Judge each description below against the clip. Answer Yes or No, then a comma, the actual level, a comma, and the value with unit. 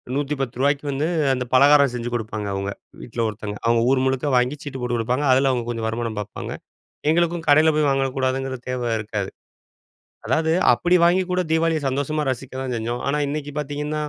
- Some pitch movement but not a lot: Yes, average, 3.6 semitones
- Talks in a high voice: No, low, 135 Hz